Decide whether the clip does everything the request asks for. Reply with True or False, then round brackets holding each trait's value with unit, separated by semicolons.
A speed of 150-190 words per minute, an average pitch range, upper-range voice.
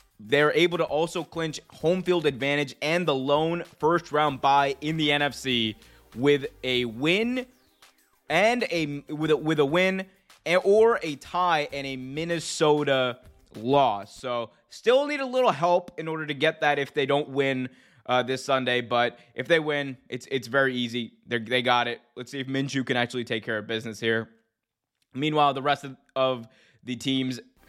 False (180 wpm; 4.2 semitones; 140 Hz)